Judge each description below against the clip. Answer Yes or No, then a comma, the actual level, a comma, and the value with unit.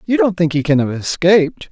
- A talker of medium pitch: Yes, medium, 165 Hz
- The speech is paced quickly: Yes, fast, 245 wpm